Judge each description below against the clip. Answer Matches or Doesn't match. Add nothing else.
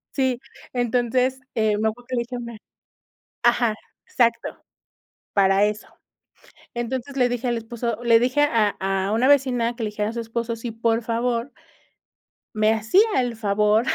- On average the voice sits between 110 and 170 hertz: Doesn't match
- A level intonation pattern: Matches